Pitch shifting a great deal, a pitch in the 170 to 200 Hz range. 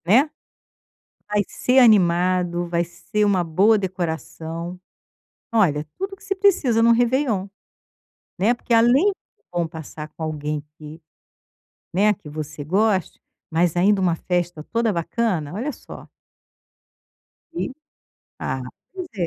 Yes: wide, 5.7 semitones; medium, 185 Hz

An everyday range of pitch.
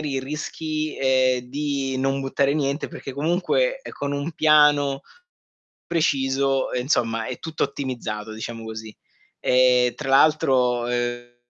Yes: average, 3.1 semitones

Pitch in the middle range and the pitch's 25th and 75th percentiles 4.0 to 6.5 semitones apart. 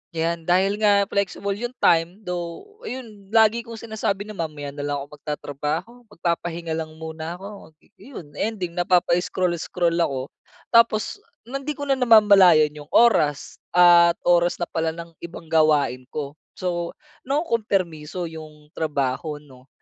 Yes: medium, 175 Hz; average, 4.7 semitones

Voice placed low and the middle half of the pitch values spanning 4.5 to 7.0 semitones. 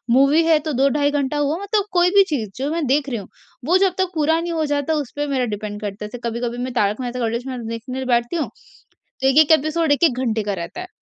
No: very high, 275 Hz; average, 4.8 semitones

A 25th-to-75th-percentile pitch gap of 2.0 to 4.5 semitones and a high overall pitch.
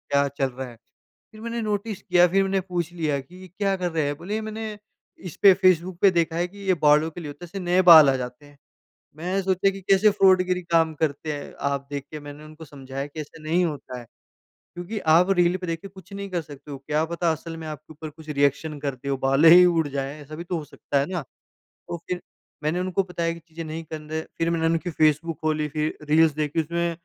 No: average, 3.3 semitones; medium, 165 Hz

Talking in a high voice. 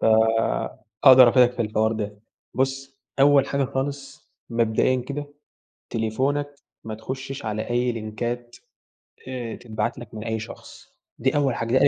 No: low, 125 Hz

